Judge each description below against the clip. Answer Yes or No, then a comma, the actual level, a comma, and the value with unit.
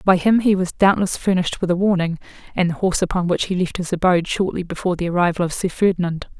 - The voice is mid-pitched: Yes, medium, 180 Hz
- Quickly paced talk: Yes, fast, 235 wpm